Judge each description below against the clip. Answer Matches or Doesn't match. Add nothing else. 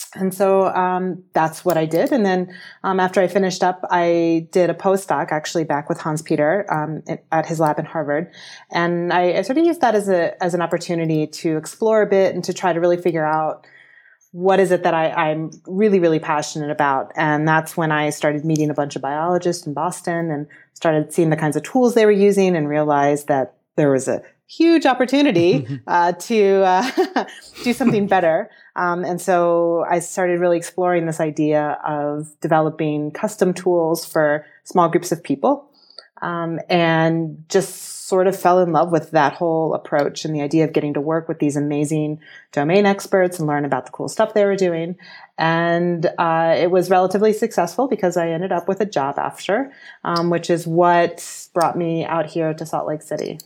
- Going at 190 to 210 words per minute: Matches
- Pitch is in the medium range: Matches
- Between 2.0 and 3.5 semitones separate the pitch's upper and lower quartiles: Matches